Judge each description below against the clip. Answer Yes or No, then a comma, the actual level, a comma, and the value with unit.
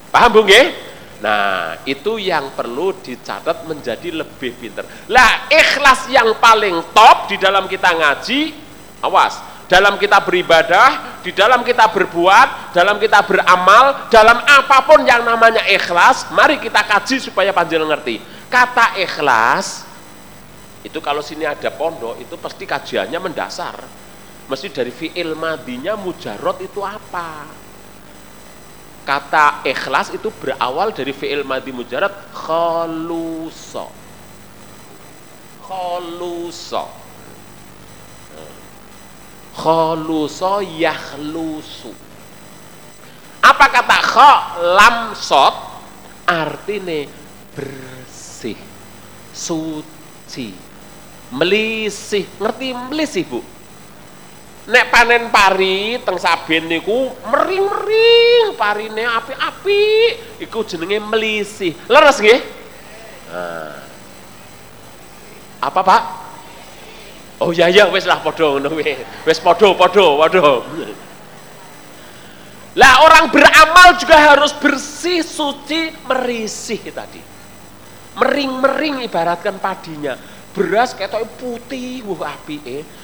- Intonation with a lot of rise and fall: Yes, wide, 8.2 semitones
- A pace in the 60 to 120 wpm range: Yes, average, 90 wpm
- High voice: Yes, high, 200 Hz